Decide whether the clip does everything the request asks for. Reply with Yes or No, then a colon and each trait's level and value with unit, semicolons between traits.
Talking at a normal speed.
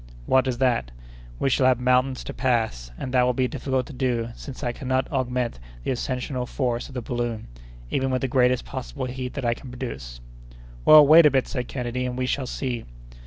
No: fast, 210 wpm